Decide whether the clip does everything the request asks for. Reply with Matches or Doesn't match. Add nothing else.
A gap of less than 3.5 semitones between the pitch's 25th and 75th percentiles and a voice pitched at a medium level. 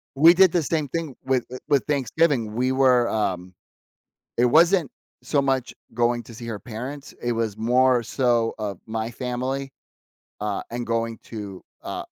Doesn't match